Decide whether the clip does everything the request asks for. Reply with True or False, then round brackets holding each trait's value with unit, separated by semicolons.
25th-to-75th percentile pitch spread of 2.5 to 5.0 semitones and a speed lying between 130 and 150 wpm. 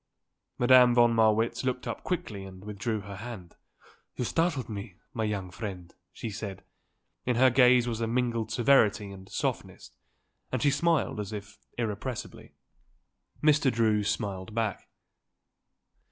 True (3.4 semitones; 140 wpm)